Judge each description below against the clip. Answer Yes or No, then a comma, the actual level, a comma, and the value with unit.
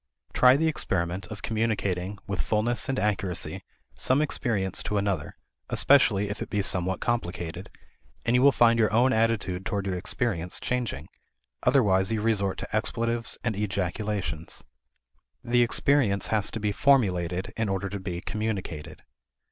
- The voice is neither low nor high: No, low, 105 Hz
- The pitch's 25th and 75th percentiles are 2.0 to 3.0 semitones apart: No, average, 3.7 semitones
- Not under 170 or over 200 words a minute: No, average, 150 wpm